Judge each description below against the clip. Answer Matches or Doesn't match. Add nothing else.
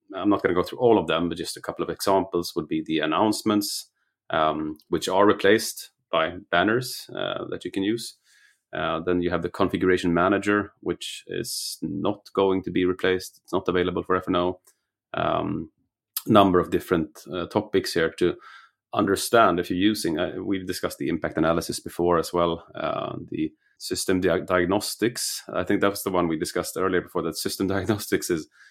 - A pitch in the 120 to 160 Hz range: Doesn't match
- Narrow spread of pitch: Doesn't match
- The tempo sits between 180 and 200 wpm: Matches